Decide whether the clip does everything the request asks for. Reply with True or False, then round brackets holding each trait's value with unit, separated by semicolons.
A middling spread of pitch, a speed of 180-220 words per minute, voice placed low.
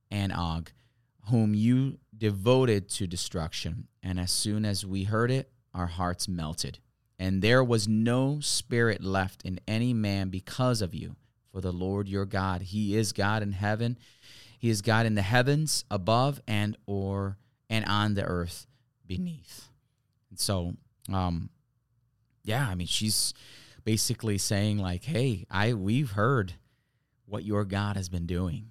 False (4.0 semitones; 150 wpm; 105 Hz)